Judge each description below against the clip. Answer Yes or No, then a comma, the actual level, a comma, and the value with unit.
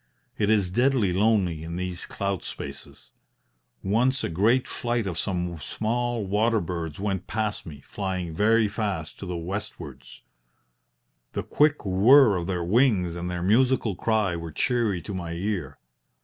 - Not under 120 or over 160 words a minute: Yes, average, 150 wpm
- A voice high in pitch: No, low, 100 Hz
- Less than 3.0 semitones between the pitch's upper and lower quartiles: No, average, 4.2 semitones